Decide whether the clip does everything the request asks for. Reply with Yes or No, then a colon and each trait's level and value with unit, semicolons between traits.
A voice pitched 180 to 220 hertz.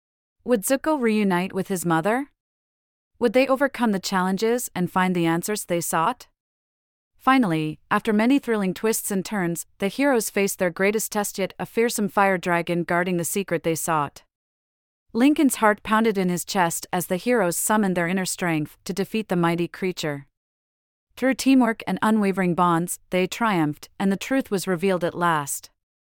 Yes: high, 190 Hz